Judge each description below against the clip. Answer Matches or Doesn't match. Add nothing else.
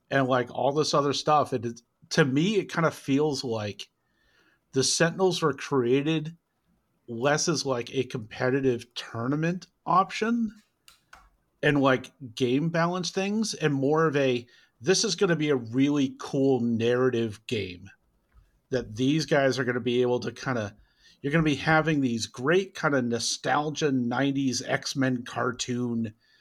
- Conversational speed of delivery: Matches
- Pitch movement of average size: Matches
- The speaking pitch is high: Doesn't match